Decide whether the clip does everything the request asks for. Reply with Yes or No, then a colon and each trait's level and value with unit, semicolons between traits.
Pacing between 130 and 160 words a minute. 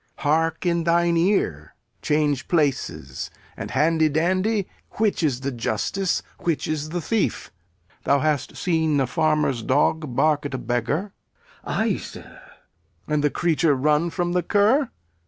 Yes: average, 150 wpm